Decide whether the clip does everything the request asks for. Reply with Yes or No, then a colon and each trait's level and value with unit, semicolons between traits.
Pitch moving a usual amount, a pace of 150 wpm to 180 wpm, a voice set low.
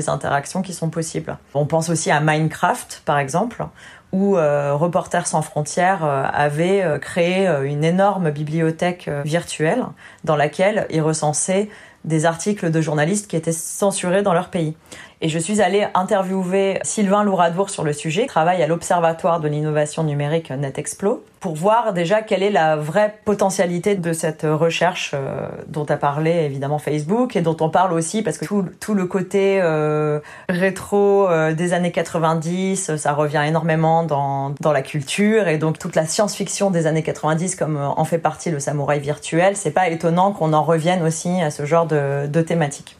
No: average, 3.8 semitones; average, 170 wpm; medium, 165 Hz